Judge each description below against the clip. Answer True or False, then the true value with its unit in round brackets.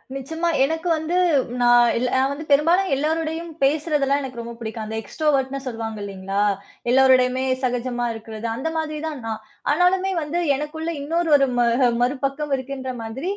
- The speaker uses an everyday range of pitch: True (4.4 semitones)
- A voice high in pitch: True (275 Hz)